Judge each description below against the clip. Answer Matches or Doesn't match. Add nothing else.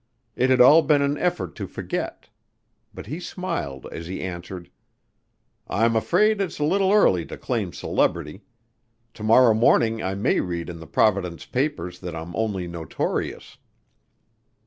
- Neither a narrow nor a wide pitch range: Doesn't match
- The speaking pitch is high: Doesn't match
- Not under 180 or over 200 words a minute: Doesn't match